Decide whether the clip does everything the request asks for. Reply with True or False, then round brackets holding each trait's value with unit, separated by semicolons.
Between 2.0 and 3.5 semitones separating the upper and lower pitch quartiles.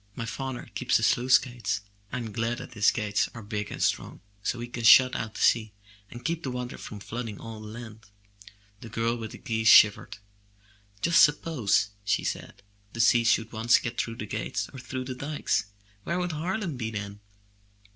True (2.7 semitones)